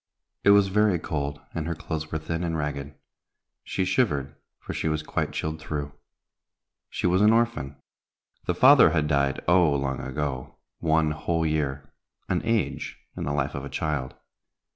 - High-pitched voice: No, very low, 80 Hz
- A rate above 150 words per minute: Yes, average, 165 wpm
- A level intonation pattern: No, average, 3.6 semitones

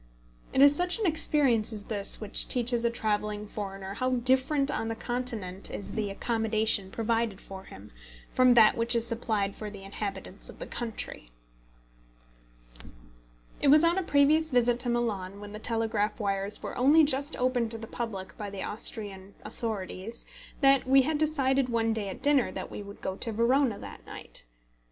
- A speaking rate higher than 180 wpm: No, average, 175 wpm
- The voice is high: Yes, high, 230 Hz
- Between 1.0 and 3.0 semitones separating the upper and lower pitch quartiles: No, average, 4.0 semitones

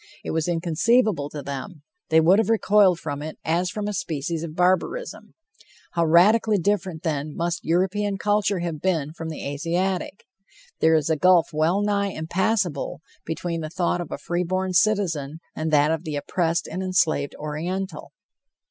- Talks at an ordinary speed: Yes, average, 165 wpm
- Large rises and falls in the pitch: No, average, 3.3 semitones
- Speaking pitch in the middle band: Yes, medium, 170 Hz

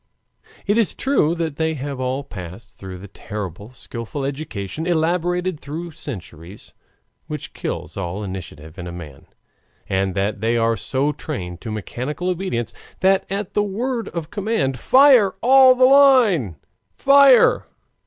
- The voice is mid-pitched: Yes, medium, 145 Hz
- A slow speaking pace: No, average, 145 wpm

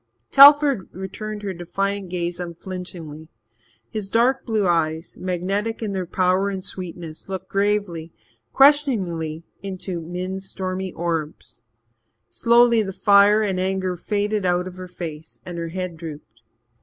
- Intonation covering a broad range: No, average, 2.9 semitones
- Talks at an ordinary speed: No, slow, 130 wpm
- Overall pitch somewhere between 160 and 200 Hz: Yes, medium, 185 Hz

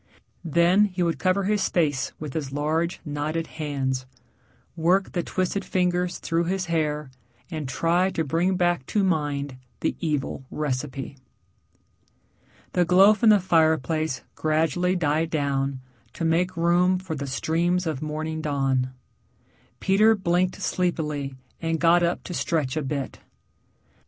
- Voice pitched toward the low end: No, medium, 165 Hz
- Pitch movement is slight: No, average, 3.5 semitones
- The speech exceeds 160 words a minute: No, slow, 135 wpm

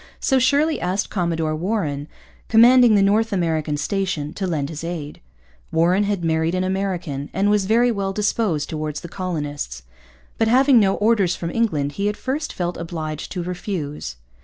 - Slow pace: No, average, 165 wpm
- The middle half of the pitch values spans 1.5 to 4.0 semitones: No, average, 4.9 semitones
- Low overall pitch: No, medium, 185 Hz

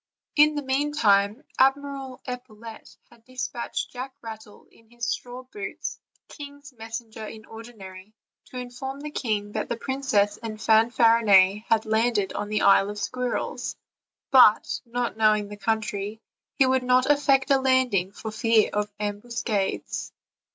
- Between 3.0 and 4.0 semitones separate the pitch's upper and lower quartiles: Yes, average, 3.6 semitones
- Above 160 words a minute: No, average, 145 wpm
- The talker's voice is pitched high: Yes, high, 230 Hz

